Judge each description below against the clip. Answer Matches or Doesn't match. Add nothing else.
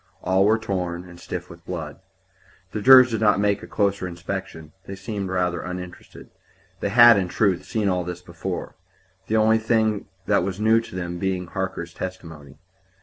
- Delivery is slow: Doesn't match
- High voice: Doesn't match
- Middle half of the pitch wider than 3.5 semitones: Doesn't match